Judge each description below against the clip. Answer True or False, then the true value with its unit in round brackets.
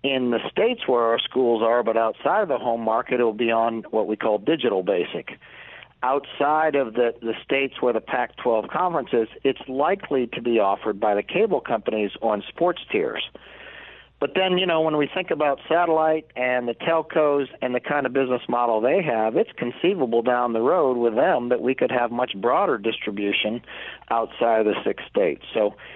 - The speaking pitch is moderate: False (125 Hz)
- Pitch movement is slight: False (3.6 semitones)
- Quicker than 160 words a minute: True (195 wpm)